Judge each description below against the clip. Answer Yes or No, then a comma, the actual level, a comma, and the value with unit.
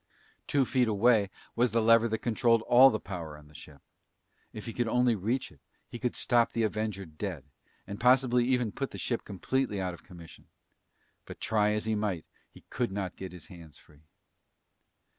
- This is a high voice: No, low, 110 Hz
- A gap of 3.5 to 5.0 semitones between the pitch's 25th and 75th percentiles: Yes, average, 4.5 semitones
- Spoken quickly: No, average, 190 wpm